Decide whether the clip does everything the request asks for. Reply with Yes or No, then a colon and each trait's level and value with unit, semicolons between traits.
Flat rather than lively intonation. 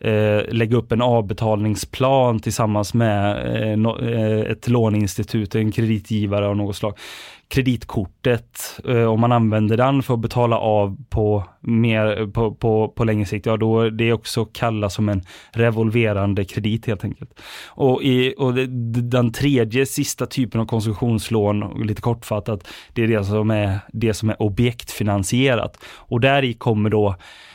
Yes: narrow, 2.1 semitones